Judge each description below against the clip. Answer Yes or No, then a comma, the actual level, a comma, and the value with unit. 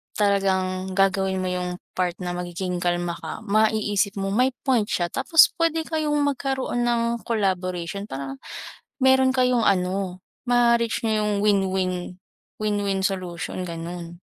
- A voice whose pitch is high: Yes, high, 195 Hz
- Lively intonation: No, average, 4.4 semitones